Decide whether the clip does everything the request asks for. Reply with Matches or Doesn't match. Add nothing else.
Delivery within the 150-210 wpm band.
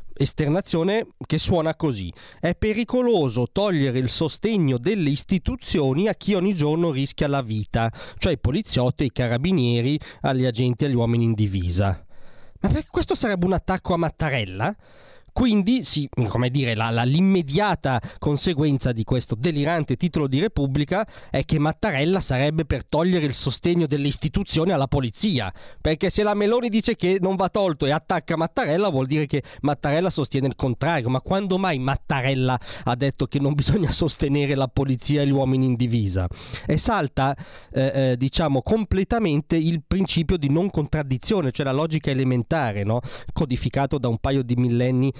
Matches